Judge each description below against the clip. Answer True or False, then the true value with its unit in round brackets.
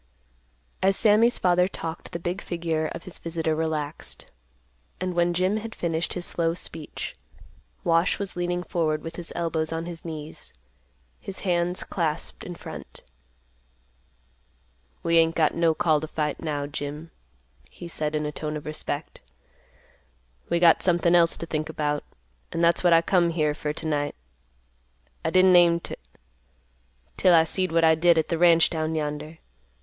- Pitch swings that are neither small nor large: False (1.9 semitones)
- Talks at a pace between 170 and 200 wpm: False (160 wpm)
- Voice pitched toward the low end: False (165 Hz)